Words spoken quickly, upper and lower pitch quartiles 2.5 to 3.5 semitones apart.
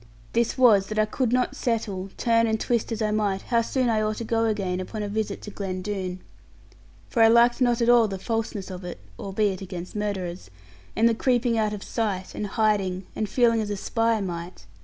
Yes: fast, 210 wpm; average, 2.9 semitones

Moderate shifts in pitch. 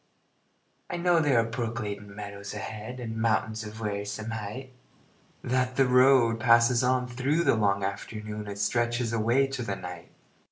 Yes: average, 3.1 semitones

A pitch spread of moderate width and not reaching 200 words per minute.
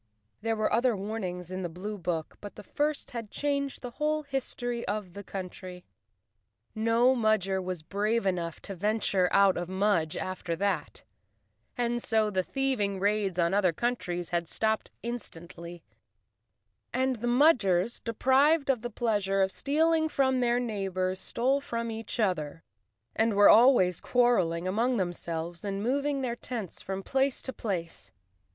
Yes: average, 4.8 semitones; average, 150 wpm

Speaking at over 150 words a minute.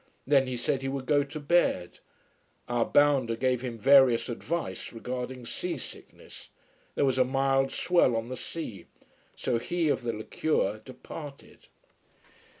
No: average, 145 wpm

